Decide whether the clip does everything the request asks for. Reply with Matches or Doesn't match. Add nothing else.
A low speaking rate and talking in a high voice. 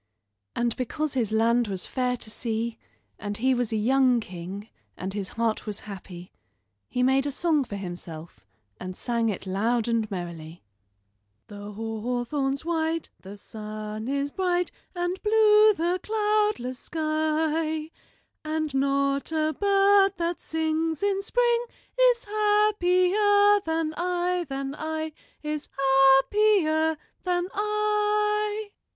Matches